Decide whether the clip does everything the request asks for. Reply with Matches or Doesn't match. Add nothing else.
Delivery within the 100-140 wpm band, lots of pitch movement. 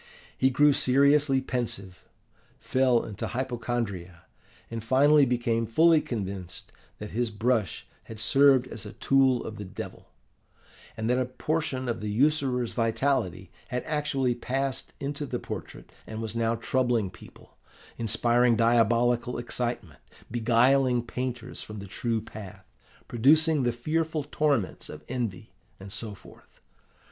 Doesn't match